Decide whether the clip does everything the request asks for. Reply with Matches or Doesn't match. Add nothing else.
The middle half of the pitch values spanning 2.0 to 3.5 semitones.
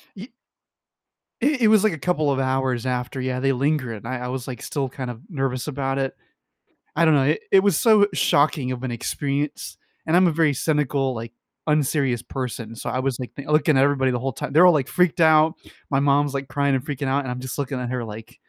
Matches